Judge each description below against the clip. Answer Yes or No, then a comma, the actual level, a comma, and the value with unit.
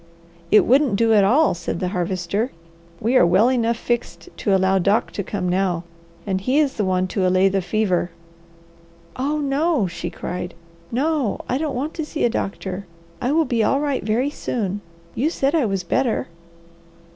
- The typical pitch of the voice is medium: No, high, 215 Hz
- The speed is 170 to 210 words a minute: Yes, average, 180 wpm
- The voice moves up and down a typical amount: No, wide, 6.2 semitones